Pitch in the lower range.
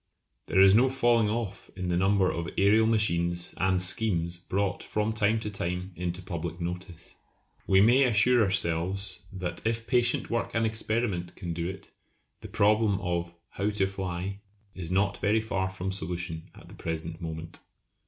Yes: very low, 95 Hz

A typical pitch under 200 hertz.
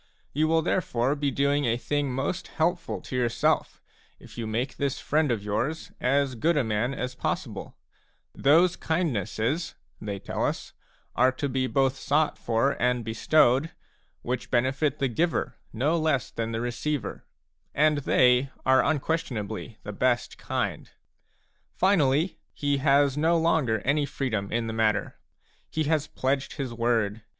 Yes: low, 135 Hz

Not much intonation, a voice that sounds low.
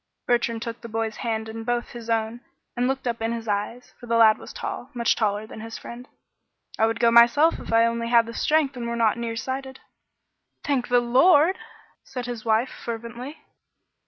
No: narrow, 1.4 semitones; high, 235 Hz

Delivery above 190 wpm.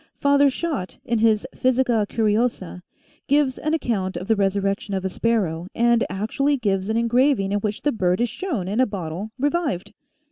No: average, 180 wpm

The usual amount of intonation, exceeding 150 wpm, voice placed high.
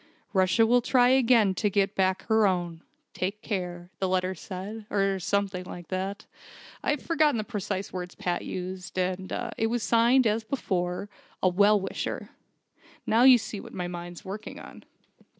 Yes: average, 3.4 semitones; average, 165 wpm; high, 195 Hz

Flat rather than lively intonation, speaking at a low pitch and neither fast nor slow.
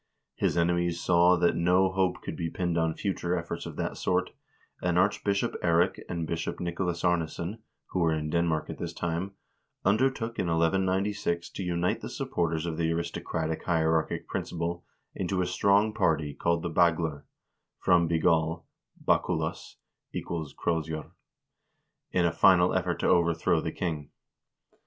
Yes: narrow, 1.6 semitones; very low, 85 Hz; average, 155 wpm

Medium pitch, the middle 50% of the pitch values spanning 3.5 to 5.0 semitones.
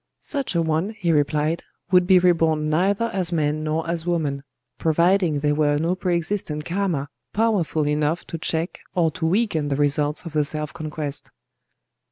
No: medium, 160 Hz; average, 3.0 semitones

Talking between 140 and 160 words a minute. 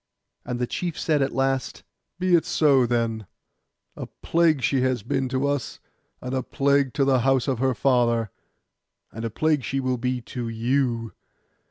No: average, 175 wpm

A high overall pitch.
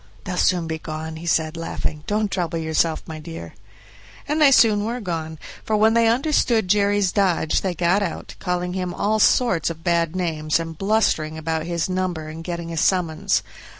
No: medium, 175 Hz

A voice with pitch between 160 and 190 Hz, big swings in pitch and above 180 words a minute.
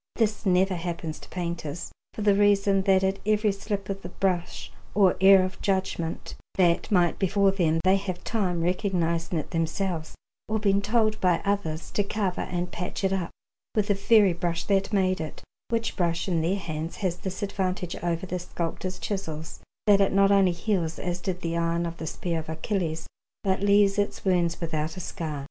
No: medium, 185 Hz; average, 2.8 semitones; average, 190 wpm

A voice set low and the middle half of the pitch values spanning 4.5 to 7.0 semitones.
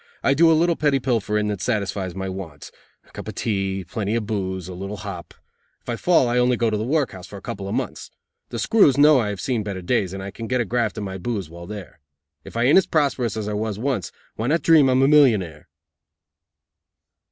Yes: low, 110 Hz; average, 4.8 semitones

